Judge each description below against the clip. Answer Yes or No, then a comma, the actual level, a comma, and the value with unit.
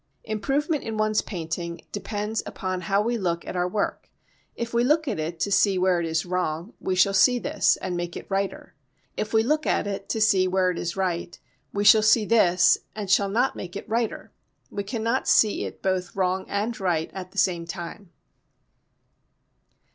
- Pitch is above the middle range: Yes, high, 195 Hz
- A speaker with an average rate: Yes, average, 190 wpm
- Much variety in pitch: No, average, 3.3 semitones